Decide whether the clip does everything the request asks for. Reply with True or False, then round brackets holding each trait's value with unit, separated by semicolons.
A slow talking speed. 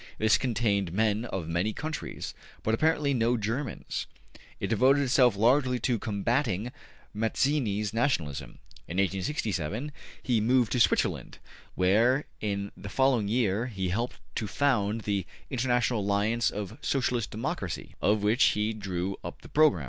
False (145 wpm)